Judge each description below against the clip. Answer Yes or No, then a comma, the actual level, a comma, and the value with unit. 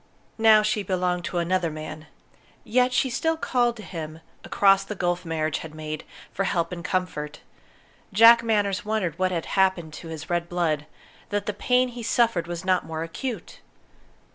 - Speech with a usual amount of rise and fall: Yes, average, 4.4 semitones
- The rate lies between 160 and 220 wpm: Yes, average, 170 wpm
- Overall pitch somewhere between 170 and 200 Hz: Yes, medium, 185 Hz